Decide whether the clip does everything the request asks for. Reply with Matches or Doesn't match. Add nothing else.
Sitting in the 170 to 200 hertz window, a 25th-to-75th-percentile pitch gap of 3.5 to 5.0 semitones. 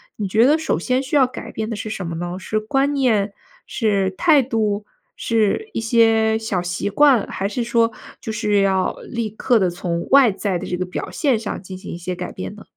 Doesn't match